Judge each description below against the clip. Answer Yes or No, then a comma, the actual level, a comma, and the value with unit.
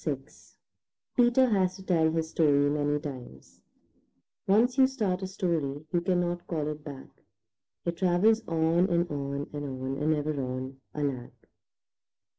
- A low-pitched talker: No, medium, 160 Hz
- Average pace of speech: Yes, average, 145 wpm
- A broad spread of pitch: No, average, 4.4 semitones